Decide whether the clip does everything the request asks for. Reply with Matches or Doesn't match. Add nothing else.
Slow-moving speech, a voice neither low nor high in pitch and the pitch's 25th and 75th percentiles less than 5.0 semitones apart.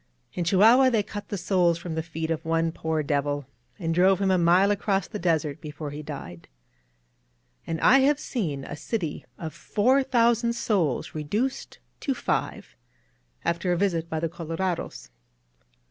Doesn't match